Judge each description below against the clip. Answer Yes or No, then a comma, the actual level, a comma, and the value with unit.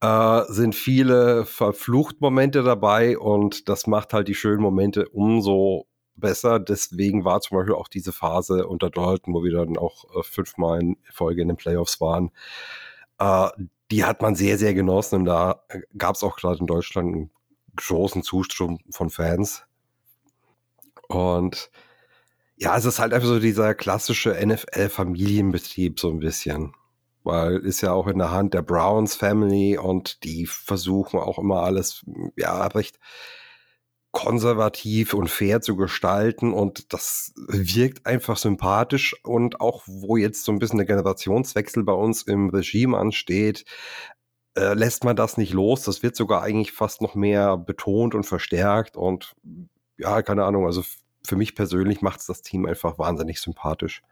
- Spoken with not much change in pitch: No, average, 3.4 semitones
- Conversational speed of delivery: Yes, average, 155 wpm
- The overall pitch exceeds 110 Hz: No, low, 100 Hz